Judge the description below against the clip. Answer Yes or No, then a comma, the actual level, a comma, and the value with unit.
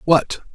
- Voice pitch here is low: No, medium, 145 Hz